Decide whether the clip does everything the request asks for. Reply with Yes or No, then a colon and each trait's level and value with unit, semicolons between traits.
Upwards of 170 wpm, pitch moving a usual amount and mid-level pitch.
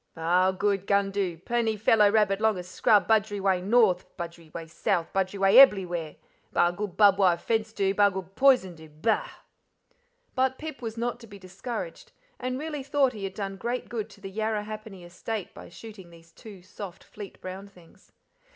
No: average, 180 wpm; average, 3.3 semitones; high, 200 Hz